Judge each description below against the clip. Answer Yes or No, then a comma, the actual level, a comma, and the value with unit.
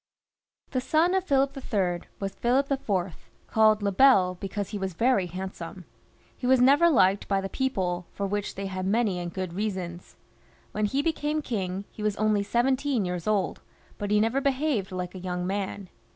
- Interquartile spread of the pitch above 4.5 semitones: Yes, wide, 5.6 semitones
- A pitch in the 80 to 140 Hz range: No, high, 205 Hz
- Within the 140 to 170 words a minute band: No, average, 185 wpm